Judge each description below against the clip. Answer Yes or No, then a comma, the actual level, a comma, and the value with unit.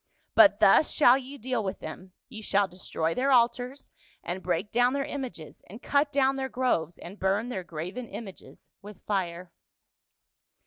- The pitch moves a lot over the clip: Yes, wide, 5.8 semitones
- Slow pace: No, average, 165 wpm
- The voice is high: Yes, high, 220 Hz